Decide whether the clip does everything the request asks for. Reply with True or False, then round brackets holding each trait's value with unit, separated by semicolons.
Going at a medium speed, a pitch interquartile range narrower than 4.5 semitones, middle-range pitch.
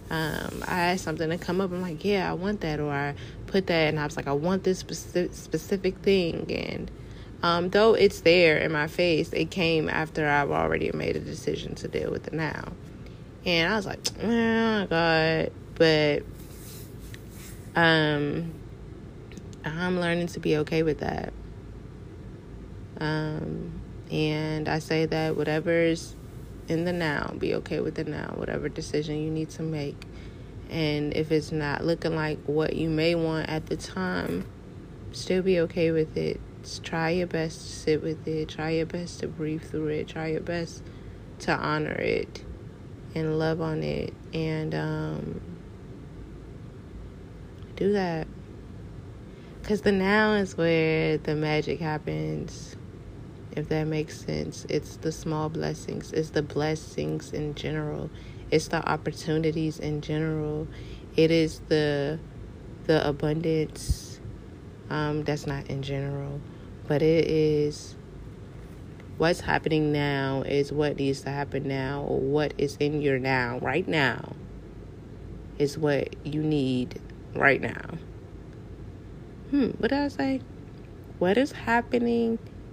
True (145 wpm; 2.8 semitones; 155 Hz)